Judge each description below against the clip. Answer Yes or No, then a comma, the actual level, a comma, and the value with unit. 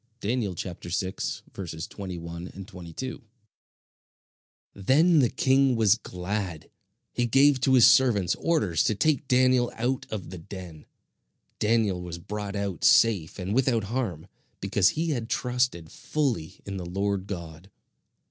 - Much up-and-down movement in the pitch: Yes, wide, 5.8 semitones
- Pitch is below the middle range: Yes, low, 100 Hz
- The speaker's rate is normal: No, slow, 130 wpm